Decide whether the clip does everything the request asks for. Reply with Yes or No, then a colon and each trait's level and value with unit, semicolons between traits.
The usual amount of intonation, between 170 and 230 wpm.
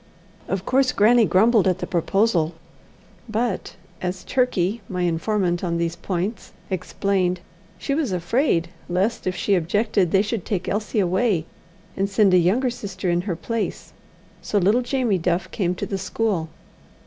No: average, 3.7 semitones; average, 155 wpm